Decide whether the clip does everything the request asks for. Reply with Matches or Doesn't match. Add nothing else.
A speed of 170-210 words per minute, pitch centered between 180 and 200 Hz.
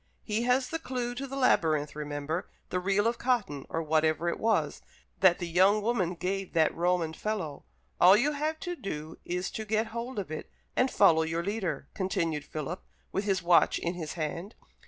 Matches